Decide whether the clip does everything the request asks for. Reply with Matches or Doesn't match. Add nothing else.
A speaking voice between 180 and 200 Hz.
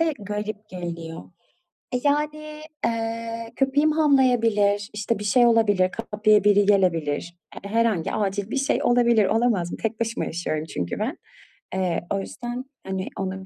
Doesn't match